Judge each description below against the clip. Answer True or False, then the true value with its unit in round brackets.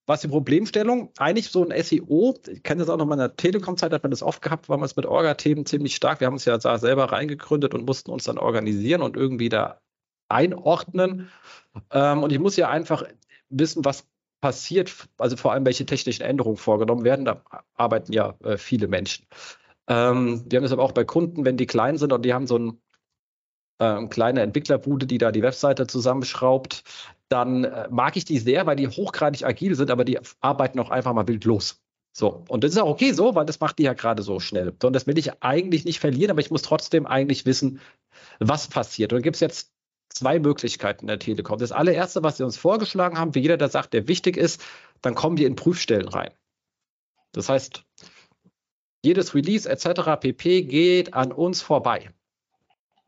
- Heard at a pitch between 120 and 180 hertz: True (140 Hz)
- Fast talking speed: True (200 wpm)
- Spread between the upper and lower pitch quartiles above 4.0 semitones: True (4.6 semitones)